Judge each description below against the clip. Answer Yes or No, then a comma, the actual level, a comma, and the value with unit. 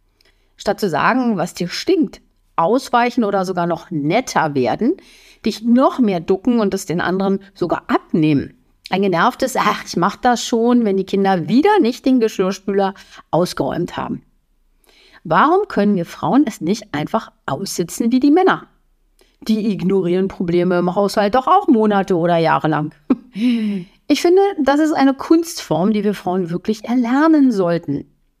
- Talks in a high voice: Yes, high, 205 Hz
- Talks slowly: No, average, 150 wpm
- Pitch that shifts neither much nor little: No, wide, 5.8 semitones